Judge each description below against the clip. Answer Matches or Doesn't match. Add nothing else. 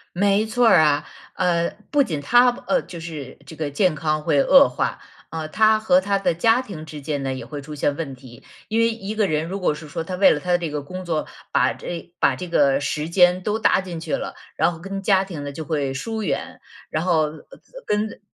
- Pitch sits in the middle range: Matches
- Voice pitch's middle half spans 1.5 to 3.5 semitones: Doesn't match